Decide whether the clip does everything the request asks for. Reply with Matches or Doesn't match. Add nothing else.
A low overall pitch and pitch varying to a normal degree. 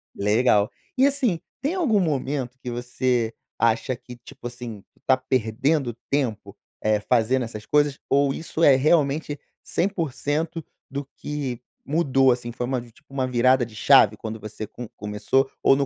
Matches